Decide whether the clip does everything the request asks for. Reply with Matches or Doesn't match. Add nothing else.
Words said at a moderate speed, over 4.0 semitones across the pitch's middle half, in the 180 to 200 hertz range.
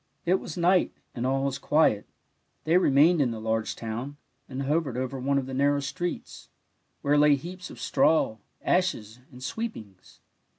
Doesn't match